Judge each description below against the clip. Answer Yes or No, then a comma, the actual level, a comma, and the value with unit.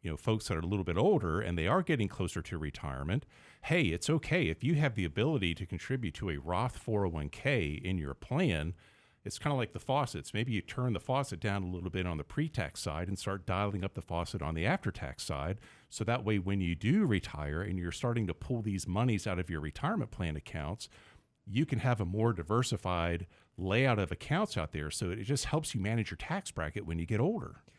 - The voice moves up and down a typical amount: No, wide, 5.7 semitones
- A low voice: Yes, low, 100 Hz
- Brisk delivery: Yes, fast, 230 wpm